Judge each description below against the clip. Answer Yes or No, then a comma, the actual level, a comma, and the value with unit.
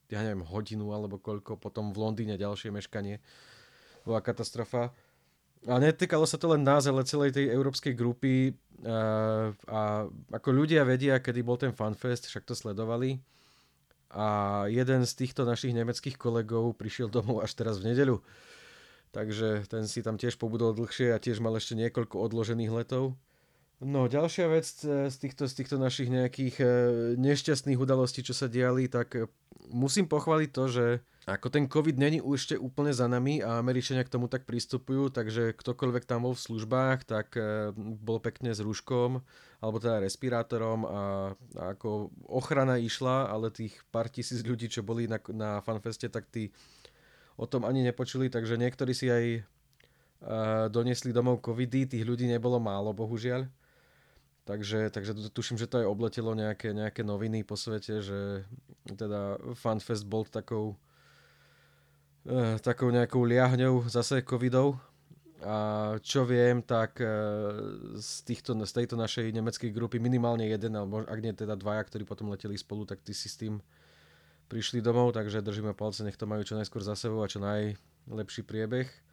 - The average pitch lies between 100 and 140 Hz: Yes, low, 115 Hz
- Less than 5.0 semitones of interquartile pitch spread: Yes, average, 2.9 semitones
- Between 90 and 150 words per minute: No, average, 160 wpm